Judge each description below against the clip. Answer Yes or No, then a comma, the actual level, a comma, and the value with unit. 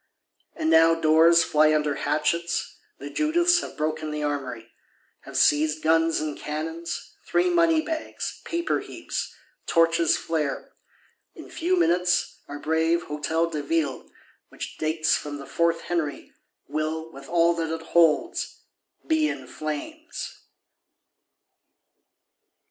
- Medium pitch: Yes, medium, 160 Hz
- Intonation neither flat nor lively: No, narrow, 2.0 semitones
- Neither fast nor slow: No, slow, 125 wpm